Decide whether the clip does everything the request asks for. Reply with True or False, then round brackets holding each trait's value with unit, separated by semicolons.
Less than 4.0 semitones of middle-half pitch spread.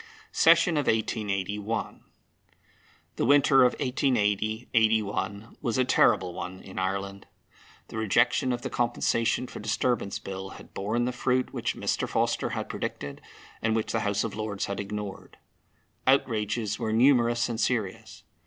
True (3.1 semitones)